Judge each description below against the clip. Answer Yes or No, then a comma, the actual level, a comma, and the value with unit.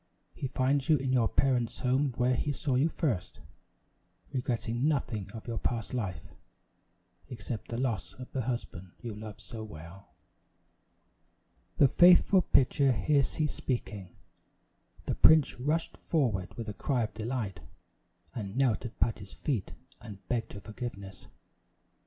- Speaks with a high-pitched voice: No, low, 120 Hz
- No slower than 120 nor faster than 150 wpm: Yes, average, 140 wpm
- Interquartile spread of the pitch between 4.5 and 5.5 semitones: No, average, 4.0 semitones